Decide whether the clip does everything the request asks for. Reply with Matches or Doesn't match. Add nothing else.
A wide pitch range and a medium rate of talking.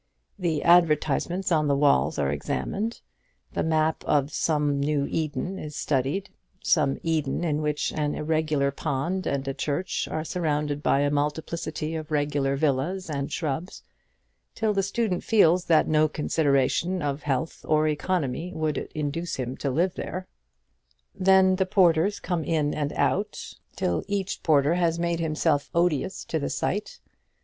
Doesn't match